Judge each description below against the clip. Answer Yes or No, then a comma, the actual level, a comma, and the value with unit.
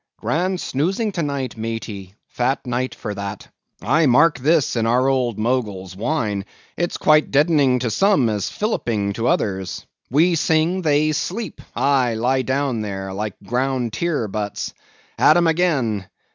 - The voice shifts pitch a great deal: Yes, wide, 6.1 semitones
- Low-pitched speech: Yes, low, 130 Hz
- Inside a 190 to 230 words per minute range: No, average, 150 wpm